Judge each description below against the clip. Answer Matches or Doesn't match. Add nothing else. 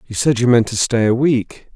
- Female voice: Doesn't match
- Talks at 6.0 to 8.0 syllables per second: Doesn't match